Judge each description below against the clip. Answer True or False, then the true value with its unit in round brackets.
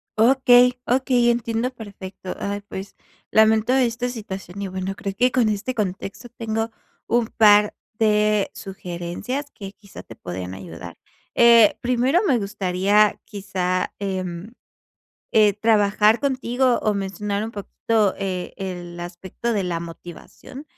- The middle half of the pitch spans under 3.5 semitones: False (3.8 semitones)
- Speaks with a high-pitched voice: True (210 Hz)